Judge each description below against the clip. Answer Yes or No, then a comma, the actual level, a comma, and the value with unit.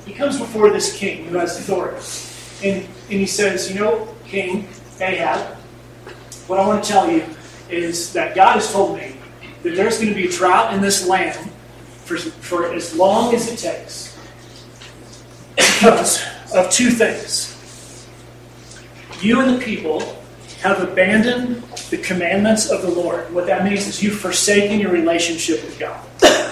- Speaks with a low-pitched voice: No, high, 190 Hz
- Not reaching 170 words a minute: Yes, average, 160 wpm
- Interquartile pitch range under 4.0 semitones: Yes, average, 3.6 semitones